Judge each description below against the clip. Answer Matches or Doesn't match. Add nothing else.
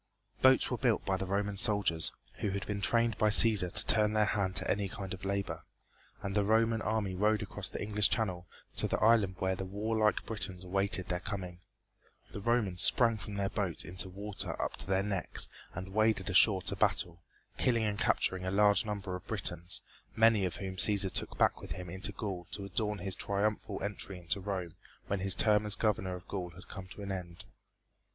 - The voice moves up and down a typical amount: Doesn't match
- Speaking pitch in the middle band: Doesn't match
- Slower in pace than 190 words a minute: Doesn't match